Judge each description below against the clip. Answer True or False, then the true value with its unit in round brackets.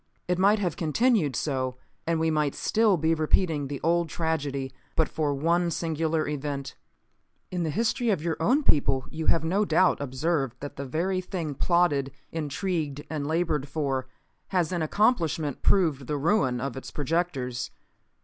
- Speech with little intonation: False (3.6 semitones)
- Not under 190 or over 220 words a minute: False (160 wpm)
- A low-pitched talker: False (160 Hz)